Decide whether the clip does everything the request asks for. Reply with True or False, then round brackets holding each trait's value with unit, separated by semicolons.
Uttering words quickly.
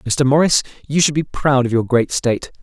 True (230 wpm)